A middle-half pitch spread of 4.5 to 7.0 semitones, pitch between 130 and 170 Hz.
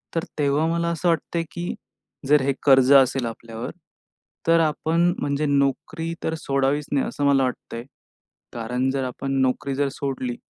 No: average, 3.1 semitones; medium, 140 Hz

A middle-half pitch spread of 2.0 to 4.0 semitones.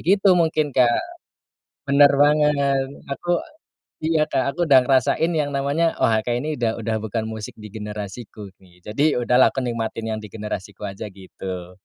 No: average, 5.3 semitones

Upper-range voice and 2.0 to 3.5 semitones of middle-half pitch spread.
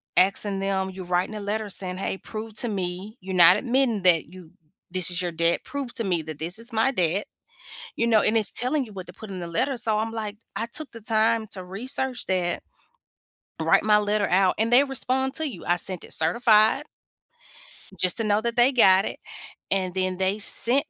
No: high, 210 Hz; average, 4.0 semitones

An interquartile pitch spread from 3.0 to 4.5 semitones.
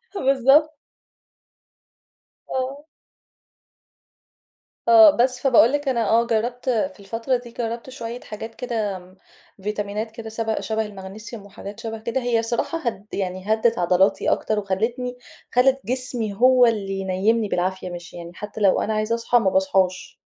Yes: average, 3.5 semitones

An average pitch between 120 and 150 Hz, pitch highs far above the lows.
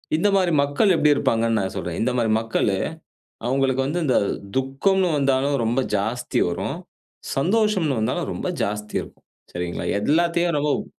Yes: low, 135 Hz; wide, 6.9 semitones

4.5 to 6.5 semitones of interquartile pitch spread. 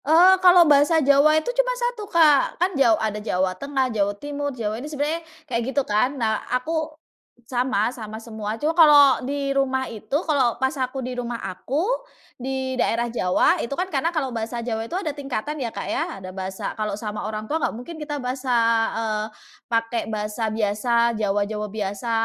Yes: average, 4.9 semitones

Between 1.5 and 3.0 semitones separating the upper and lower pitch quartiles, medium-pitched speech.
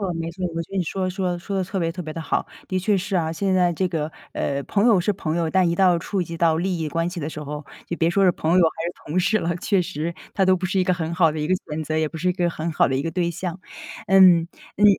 Yes: narrow, 2.4 semitones; medium, 175 Hz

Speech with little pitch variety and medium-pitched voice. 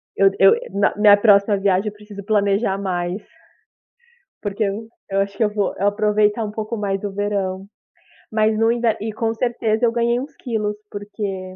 No: narrow, 1.7 semitones; high, 210 Hz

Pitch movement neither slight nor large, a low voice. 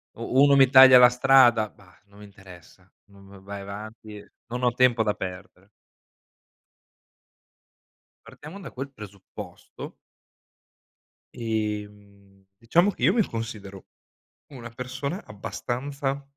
Yes: average, 4.6 semitones; low, 110 Hz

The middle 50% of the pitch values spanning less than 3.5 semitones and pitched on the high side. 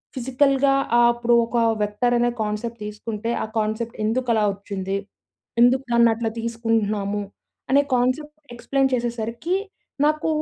Yes: average, 2.8 semitones; high, 235 Hz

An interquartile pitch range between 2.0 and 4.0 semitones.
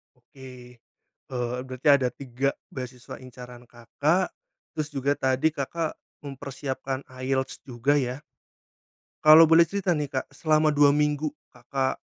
Yes: average, 2.8 semitones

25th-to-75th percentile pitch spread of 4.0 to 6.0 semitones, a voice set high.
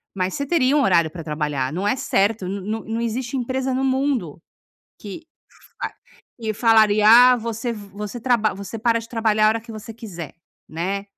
No: average, 3.6 semitones; high, 220 Hz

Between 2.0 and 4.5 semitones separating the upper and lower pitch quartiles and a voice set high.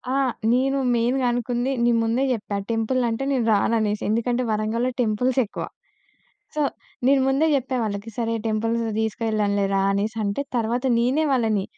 Yes: average, 2.7 semitones; high, 230 Hz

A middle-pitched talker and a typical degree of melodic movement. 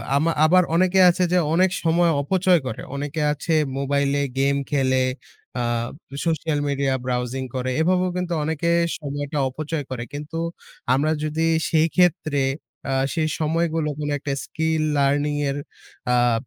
Yes: medium, 150 Hz; average, 3.0 semitones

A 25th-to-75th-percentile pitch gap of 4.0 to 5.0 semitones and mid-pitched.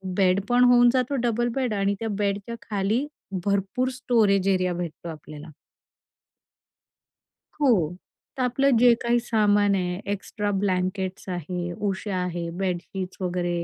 No: average, 4.5 semitones; high, 200 Hz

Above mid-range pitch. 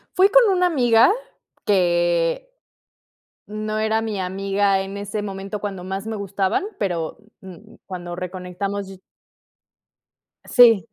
Yes: high, 195 Hz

